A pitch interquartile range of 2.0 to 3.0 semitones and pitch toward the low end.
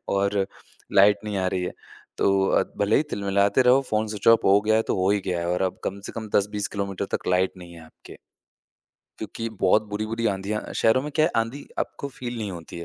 Yes: narrow, 2.6 semitones; low, 100 Hz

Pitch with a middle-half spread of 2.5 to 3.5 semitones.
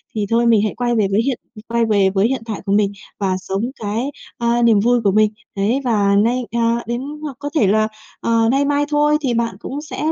Yes: average, 3.1 semitones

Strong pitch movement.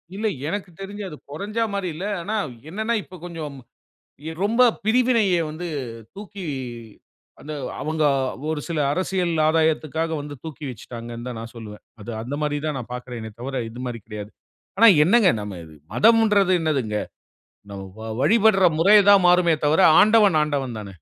Yes: wide, 8.2 semitones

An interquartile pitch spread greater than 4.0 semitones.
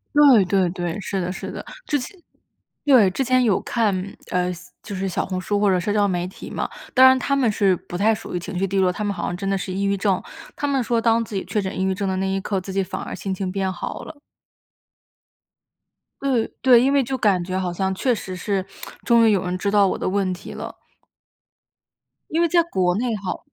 No: average, 3.7 semitones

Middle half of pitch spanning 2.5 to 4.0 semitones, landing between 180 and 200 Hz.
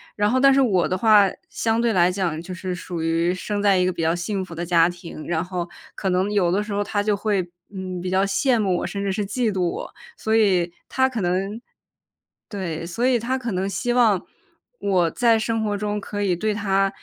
Yes: average, 3.1 semitones; high, 195 Hz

